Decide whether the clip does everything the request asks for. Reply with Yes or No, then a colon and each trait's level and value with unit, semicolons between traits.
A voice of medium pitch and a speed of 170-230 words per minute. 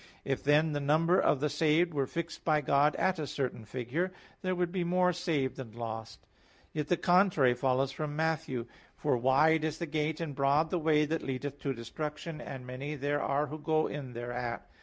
Yes: medium, 150 Hz; average, 200 wpm